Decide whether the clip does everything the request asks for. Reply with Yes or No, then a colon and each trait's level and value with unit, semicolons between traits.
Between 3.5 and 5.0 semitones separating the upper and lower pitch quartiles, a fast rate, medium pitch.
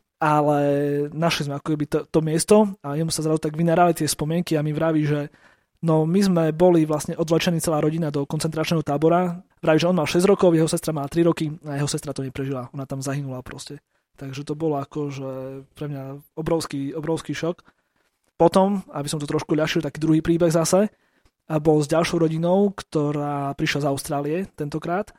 No: narrow, 2.5 semitones; fast, 195 wpm; medium, 155 Hz